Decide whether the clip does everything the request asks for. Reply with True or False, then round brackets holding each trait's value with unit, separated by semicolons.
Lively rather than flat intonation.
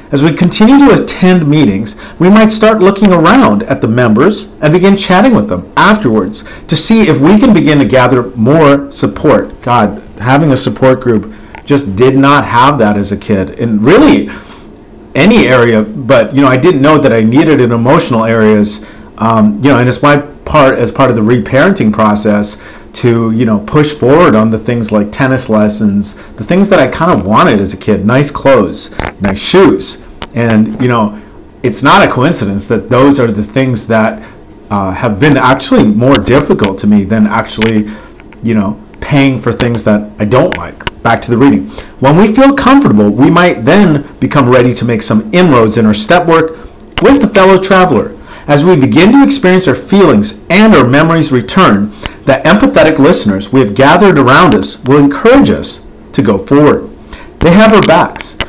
True (6.1 semitones)